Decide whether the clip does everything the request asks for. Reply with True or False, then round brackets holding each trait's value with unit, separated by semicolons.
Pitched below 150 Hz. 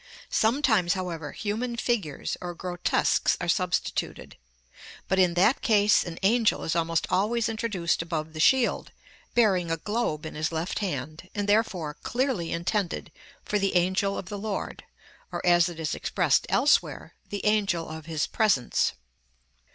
False (185 Hz)